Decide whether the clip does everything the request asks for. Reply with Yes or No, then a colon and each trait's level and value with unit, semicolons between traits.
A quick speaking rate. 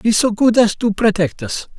Yes: fast, 235 wpm